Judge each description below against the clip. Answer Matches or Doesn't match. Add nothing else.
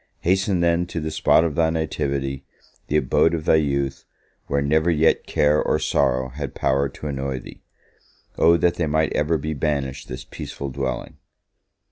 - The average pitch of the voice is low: Matches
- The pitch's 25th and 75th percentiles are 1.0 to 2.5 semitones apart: Doesn't match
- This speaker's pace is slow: Doesn't match